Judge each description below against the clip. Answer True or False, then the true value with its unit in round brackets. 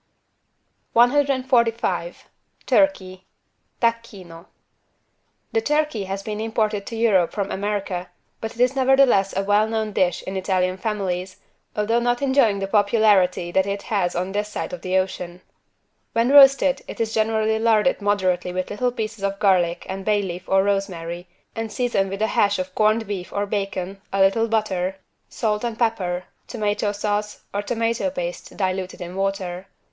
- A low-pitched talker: False (205 Hz)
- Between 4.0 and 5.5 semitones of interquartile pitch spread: False (3.1 semitones)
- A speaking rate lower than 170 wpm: True (155 wpm)